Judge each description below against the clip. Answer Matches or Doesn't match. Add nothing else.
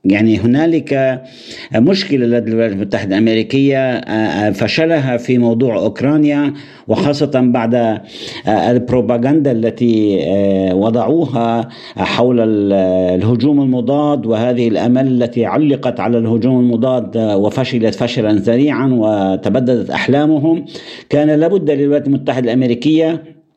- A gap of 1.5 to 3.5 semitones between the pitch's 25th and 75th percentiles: Doesn't match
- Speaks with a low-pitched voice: Matches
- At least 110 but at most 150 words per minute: Doesn't match